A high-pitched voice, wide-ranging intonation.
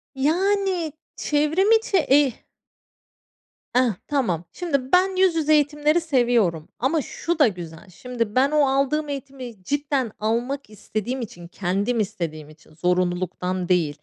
Yes: very high, 260 Hz; wide, 8.3 semitones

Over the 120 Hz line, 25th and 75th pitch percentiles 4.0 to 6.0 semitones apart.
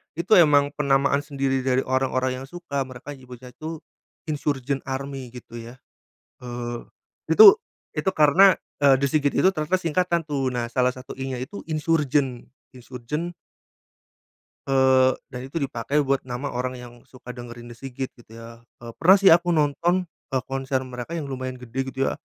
No: low, 135 Hz; average, 2.9 semitones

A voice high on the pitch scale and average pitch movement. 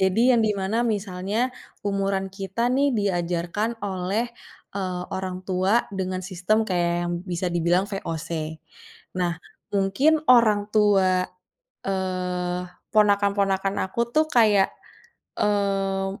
No: high, 195 Hz; narrow, 1.9 semitones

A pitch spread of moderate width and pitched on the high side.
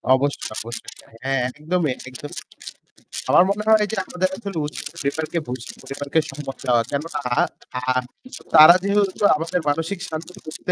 No: average, 4.6 semitones; medium, 155 Hz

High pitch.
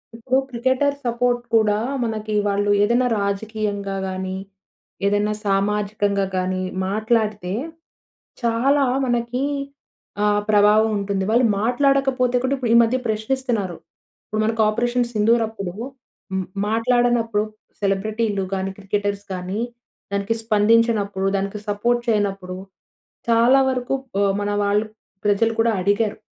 Yes: high, 215 Hz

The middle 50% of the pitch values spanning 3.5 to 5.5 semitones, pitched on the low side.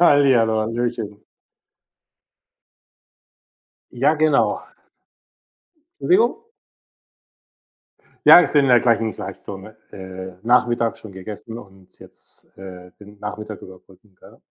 Yes: average, 4.1 semitones; low, 110 Hz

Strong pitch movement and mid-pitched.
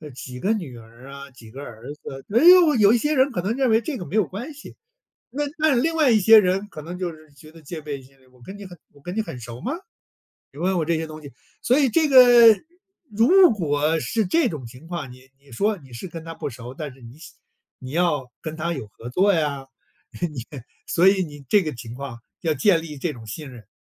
Yes: wide, 8.0 semitones; medium, 165 Hz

